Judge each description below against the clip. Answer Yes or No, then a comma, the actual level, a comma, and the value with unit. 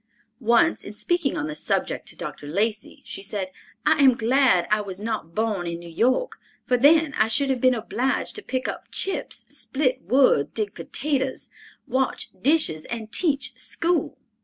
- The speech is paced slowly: No, average, 170 wpm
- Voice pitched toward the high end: Yes, high, 240 Hz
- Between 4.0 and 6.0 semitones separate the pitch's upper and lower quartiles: Yes, average, 4.9 semitones